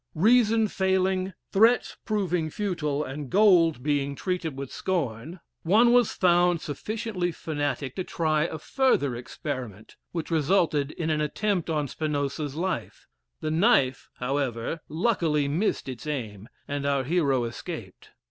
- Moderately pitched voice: Yes, medium, 155 Hz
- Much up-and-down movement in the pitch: No, average, 5.0 semitones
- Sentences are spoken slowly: Yes, slow, 130 wpm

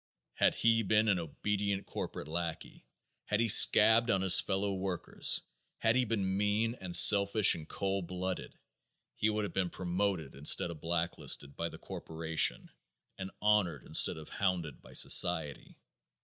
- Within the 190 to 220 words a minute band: No, average, 150 wpm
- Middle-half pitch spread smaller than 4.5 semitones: Yes, average, 3.6 semitones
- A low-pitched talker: Yes, very low, 95 Hz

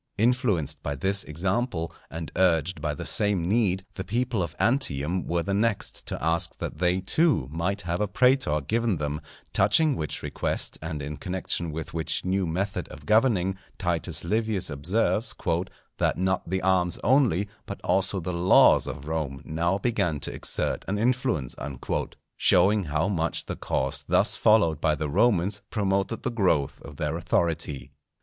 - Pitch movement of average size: Yes, average, 4.5 semitones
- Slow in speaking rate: No, average, 160 wpm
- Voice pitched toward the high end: No, very low, 90 Hz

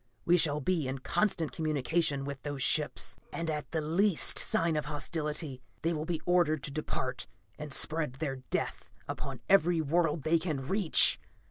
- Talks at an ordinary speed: Yes, average, 165 wpm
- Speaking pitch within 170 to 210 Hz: No, medium, 155 Hz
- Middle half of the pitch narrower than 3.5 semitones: Yes, average, 2.7 semitones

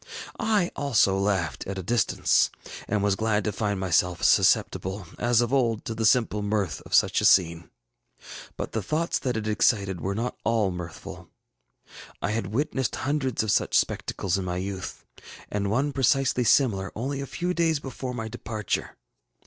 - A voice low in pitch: Yes, low, 110 Hz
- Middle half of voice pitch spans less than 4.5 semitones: No, average, 4.8 semitones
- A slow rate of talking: No, average, 170 wpm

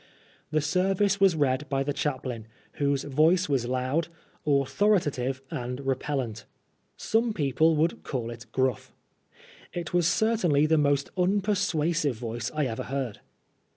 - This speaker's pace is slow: Yes, slow, 130 wpm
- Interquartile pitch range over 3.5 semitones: Yes, average, 4.8 semitones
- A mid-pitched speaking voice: Yes, medium, 145 Hz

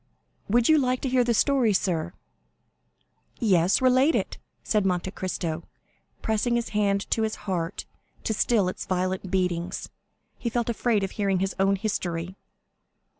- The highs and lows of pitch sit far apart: No, average, 4.3 semitones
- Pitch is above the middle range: Yes, high, 200 Hz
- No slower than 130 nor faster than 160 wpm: Yes, average, 150 wpm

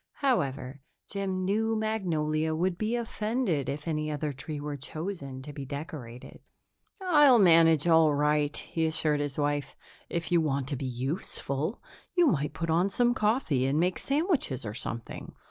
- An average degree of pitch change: No, wide, 5.7 semitones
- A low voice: No, medium, 160 Hz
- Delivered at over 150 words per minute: Yes, average, 160 wpm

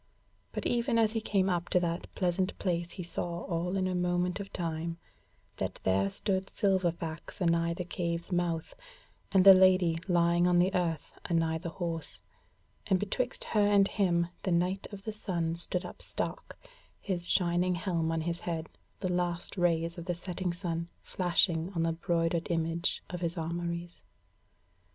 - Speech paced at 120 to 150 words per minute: No, average, 170 wpm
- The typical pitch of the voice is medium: Yes, medium, 175 Hz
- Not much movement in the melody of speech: Yes, narrow, 1.8 semitones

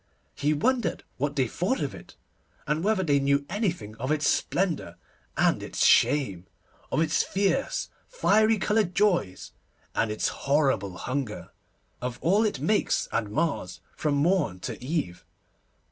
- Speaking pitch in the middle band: Yes, medium, 150 Hz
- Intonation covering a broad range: Yes, wide, 7.3 semitones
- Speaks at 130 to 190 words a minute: Yes, average, 145 wpm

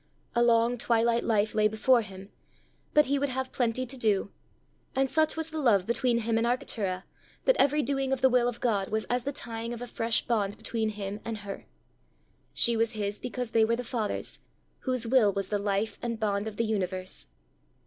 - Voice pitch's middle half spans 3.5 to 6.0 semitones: No, average, 3.0 semitones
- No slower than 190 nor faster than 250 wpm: Yes, fast, 205 wpm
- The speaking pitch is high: Yes, high, 230 Hz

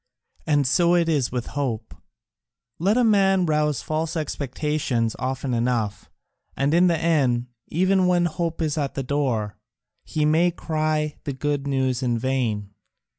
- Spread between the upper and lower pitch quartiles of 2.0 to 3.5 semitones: No, average, 4.4 semitones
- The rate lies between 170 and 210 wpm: No, average, 150 wpm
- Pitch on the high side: No, medium, 145 Hz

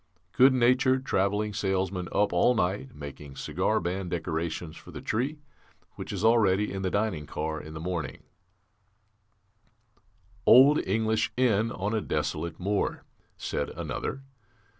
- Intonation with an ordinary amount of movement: Yes, average, 4.1 semitones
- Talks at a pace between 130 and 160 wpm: Yes, average, 140 wpm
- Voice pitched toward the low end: Yes, low, 100 Hz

